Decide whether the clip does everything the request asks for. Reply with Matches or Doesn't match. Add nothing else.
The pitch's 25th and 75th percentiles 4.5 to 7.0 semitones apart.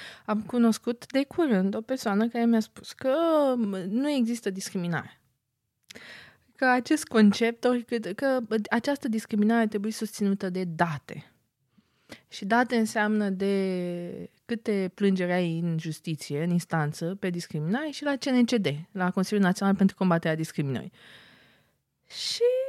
Matches